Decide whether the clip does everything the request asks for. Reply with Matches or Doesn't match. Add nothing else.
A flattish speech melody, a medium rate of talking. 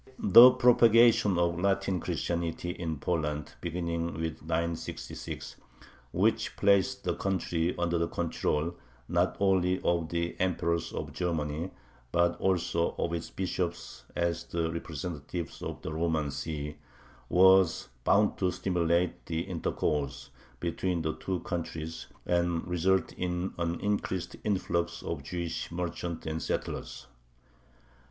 Doesn't match